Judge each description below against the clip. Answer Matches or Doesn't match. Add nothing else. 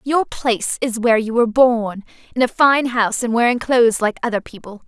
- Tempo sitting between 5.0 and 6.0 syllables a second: Matches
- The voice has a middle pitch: Doesn't match